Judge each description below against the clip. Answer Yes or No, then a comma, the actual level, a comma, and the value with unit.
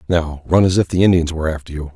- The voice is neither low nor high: No, very low, 85 Hz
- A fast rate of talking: Yes, fast, 275 wpm